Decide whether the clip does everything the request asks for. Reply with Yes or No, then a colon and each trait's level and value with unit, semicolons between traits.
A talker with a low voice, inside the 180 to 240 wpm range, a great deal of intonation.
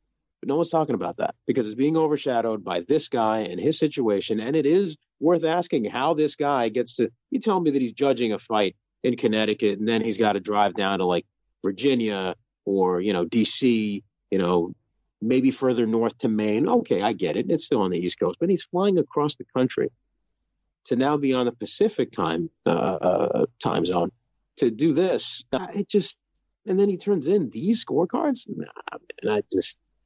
Yes: low, 130 Hz; average, 200 wpm; wide, 7.5 semitones